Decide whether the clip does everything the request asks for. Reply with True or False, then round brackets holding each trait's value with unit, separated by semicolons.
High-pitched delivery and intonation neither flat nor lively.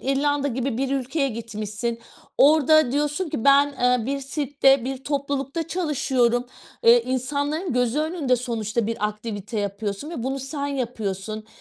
True (265 Hz; 3.8 semitones)